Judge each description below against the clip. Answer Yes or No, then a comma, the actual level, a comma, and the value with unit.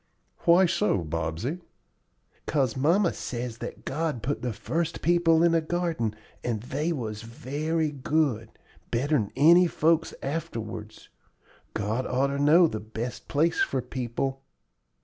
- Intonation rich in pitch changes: Yes, wide, 5.9 semitones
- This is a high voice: No, medium, 140 Hz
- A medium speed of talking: No, slow, 130 wpm